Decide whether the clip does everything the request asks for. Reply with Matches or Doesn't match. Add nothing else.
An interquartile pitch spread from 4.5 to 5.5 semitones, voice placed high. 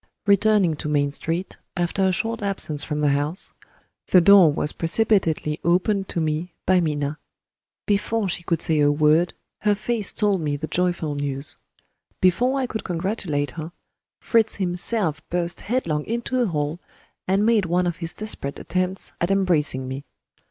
Doesn't match